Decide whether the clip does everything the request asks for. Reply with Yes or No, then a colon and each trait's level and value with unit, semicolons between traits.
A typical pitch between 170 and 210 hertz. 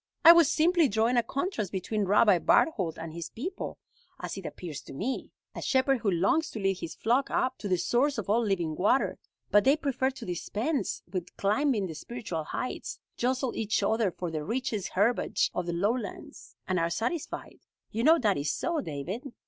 No: high, 220 Hz